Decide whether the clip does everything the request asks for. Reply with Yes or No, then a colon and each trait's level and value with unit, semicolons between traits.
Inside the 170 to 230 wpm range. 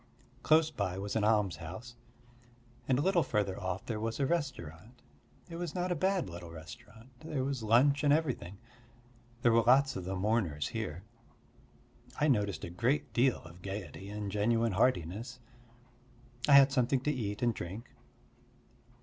No: average, 160 wpm